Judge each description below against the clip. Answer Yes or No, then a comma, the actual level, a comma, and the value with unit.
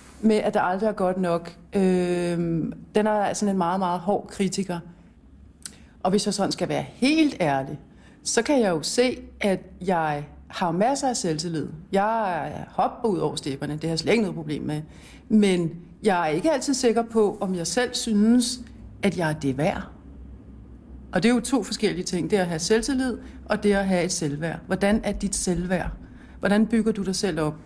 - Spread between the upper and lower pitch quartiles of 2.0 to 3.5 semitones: No, average, 4.2 semitones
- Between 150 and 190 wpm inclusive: No, average, 200 wpm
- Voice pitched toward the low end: No, high, 195 Hz